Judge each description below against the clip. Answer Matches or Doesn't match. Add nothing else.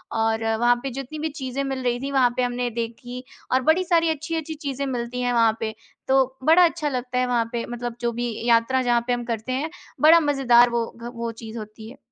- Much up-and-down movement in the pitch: Doesn't match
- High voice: Matches